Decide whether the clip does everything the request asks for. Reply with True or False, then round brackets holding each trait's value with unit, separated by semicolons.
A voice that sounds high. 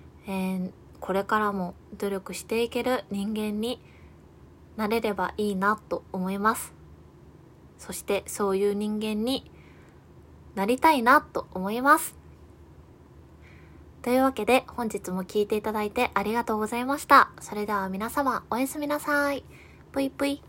True (215 Hz)